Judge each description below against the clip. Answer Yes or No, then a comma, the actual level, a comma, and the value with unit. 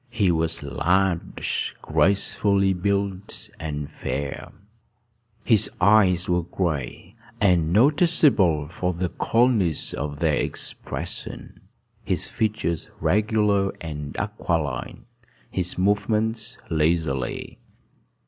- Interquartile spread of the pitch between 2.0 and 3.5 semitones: No, average, 4.3 semitones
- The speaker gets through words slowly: Yes, slow, 90 wpm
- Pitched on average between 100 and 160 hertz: No, very low, 90 Hz